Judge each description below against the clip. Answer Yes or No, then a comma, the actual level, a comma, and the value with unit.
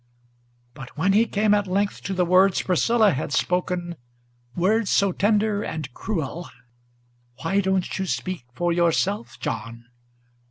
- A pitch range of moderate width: Yes, average, 3.2 semitones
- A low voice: No, medium, 185 Hz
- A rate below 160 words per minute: Yes, slow, 135 wpm